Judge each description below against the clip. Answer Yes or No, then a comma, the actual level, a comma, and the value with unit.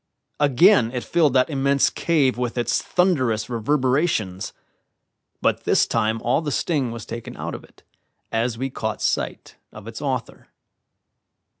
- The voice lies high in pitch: No, low, 125 Hz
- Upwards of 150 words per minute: No, average, 145 wpm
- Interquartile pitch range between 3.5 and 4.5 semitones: Yes, average, 4.1 semitones